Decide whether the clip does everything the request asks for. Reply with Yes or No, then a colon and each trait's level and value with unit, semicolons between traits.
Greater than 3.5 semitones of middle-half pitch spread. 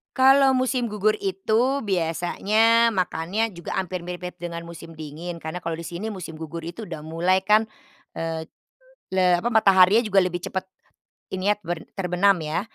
Yes: average, 4.0 semitones